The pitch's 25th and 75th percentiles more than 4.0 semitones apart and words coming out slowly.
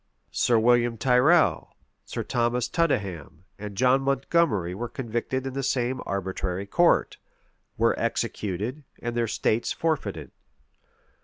Yes: average, 4.8 semitones; slow, 125 wpm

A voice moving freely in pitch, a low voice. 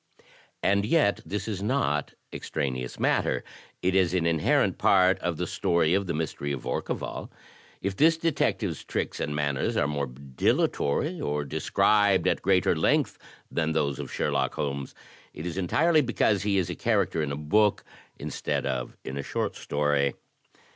Yes: wide, 5.7 semitones; very low, 85 Hz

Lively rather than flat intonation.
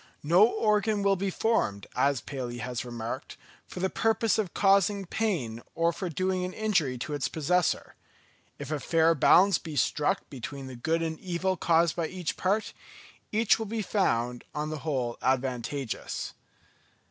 Yes: wide, 6.5 semitones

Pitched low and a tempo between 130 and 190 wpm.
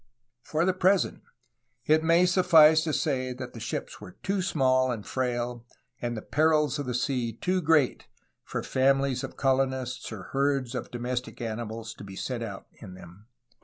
Yes: low, 130 Hz; average, 175 wpm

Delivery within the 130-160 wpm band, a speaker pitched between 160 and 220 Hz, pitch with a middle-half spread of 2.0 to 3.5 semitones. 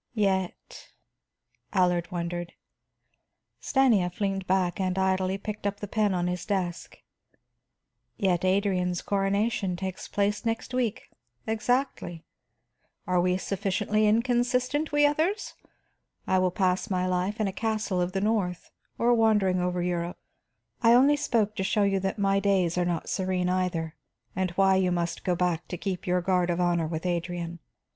Yes: average, 155 wpm; high, 190 Hz; average, 2.9 semitones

